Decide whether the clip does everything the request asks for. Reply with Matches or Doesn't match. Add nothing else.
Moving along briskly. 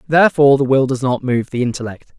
Matches